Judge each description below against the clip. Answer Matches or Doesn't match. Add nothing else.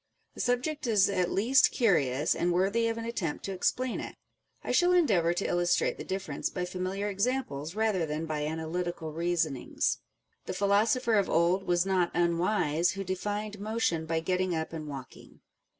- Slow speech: Doesn't match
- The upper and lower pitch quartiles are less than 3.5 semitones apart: Doesn't match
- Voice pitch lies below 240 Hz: Matches